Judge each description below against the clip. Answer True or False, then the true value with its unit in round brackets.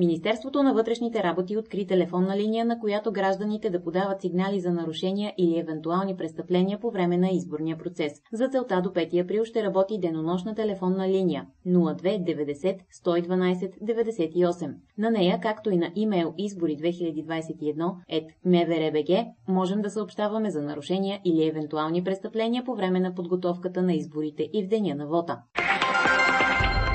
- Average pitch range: True (3.9 semitones)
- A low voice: False (180 Hz)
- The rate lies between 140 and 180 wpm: True (145 wpm)